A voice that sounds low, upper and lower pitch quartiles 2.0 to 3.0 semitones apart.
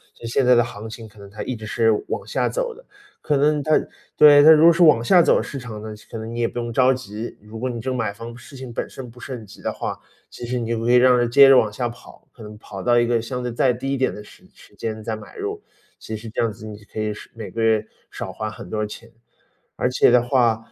Yes: low, 120 Hz; average, 2.7 semitones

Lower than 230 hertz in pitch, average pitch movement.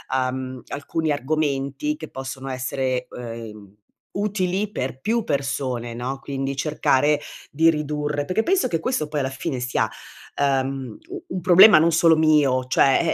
Yes: medium, 140 Hz; average, 3.8 semitones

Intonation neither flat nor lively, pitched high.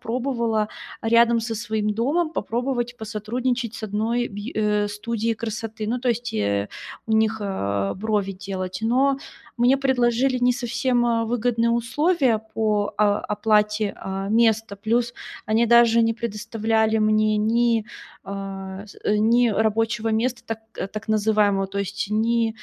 No: narrow, 2.1 semitones; high, 220 Hz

